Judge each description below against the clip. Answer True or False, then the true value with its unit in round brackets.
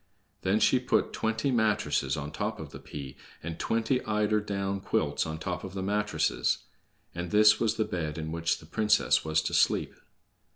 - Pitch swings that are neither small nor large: True (5.0 semitones)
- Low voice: True (100 Hz)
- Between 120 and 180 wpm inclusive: False (190 wpm)